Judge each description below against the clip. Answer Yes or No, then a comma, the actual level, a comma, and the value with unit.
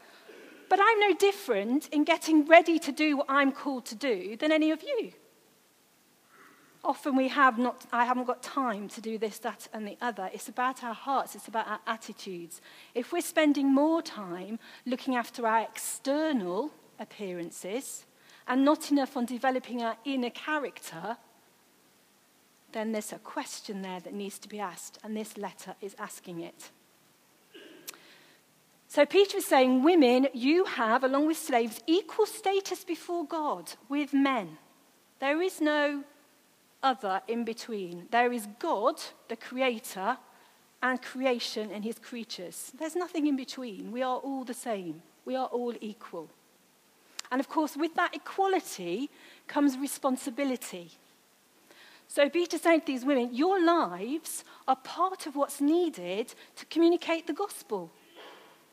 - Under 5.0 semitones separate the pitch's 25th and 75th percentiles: No, wide, 5.5 semitones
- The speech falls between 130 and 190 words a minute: Yes, average, 150 wpm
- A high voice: Yes, very high, 265 Hz